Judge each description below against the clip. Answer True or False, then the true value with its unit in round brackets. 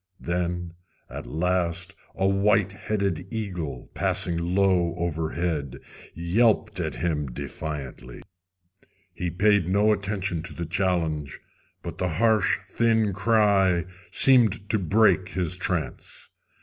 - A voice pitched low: True (90 Hz)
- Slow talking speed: True (110 wpm)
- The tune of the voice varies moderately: True (3.2 semitones)